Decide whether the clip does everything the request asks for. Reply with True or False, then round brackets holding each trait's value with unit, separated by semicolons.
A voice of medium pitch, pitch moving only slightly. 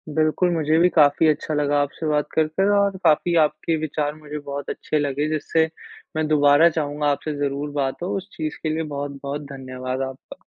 True (150 Hz; 1.8 semitones)